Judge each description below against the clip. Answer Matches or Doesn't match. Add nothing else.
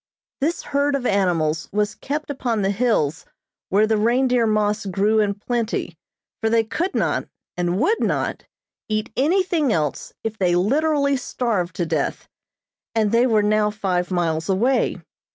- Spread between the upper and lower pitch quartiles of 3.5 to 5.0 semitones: Matches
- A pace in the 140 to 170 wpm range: Matches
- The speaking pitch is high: Matches